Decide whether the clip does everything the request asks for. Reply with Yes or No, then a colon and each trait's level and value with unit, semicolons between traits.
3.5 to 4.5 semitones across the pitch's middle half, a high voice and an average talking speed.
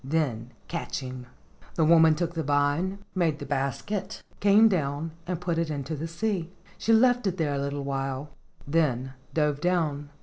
No: average, 3.8 semitones; medium, 155 Hz; average, 170 wpm